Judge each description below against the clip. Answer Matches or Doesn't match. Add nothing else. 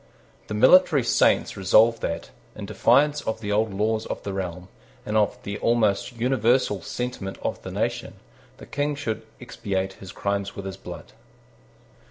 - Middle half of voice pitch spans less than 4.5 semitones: Matches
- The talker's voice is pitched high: Doesn't match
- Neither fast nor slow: Matches